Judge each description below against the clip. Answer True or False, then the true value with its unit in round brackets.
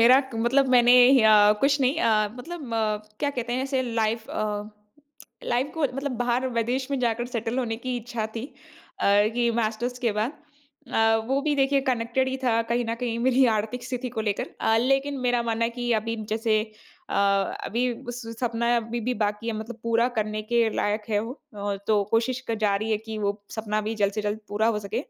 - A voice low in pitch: False (235 Hz)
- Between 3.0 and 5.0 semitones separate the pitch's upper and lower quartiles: False (2.5 semitones)